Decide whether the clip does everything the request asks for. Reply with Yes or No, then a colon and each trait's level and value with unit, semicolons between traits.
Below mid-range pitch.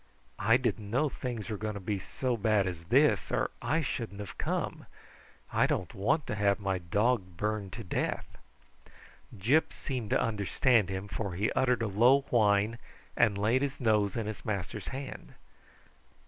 Yes: low, 105 Hz